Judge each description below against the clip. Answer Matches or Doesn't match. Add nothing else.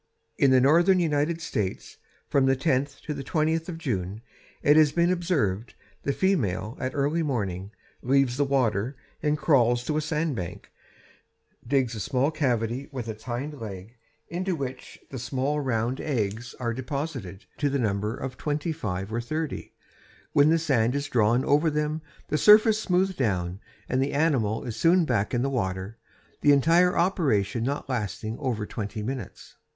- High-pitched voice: Doesn't match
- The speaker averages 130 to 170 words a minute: Matches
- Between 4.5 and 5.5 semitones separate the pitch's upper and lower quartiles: Matches